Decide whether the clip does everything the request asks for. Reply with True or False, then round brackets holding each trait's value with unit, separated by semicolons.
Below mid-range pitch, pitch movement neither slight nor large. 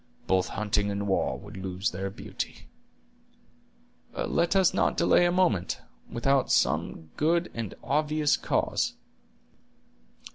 False (115 Hz; 8.2 semitones)